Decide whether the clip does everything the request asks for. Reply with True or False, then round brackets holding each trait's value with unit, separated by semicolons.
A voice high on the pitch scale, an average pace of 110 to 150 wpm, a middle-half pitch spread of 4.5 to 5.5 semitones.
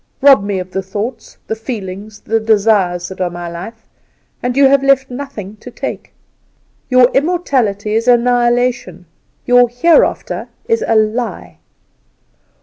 False (225 Hz; 140 wpm; 3.9 semitones)